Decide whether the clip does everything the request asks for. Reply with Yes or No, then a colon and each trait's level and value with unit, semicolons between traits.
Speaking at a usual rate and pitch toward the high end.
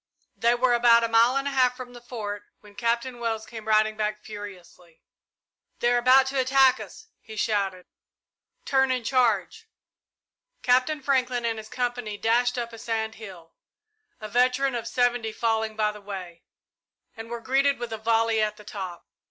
Yes: average, 175 wpm; high, 230 Hz